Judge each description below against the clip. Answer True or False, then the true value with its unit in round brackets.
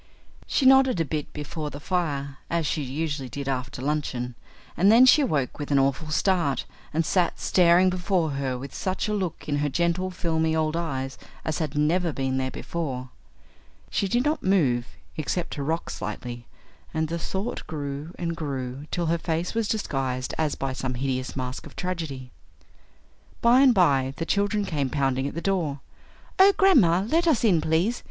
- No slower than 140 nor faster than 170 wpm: False (180 wpm)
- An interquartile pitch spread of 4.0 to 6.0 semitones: True (5.0 semitones)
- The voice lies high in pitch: False (160 Hz)